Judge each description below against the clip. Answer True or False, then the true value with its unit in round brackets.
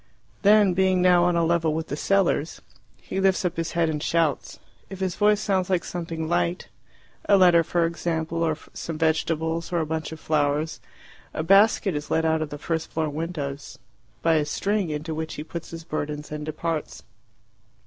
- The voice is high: False (165 Hz)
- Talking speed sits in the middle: True (190 wpm)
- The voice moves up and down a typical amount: False (2.2 semitones)